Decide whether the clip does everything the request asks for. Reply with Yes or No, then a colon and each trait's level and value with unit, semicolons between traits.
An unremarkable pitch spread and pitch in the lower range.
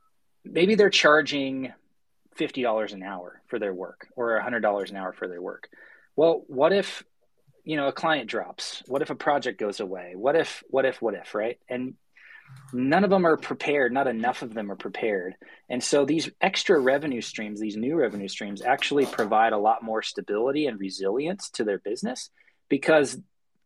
No: wide, 6.5 semitones; low, 125 Hz